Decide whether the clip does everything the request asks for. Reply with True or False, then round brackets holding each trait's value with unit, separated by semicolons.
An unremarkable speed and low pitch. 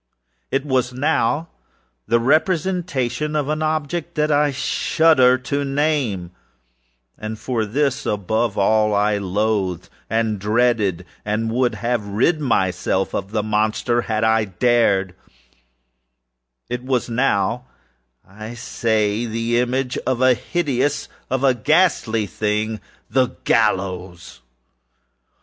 False (110 wpm; 115 Hz)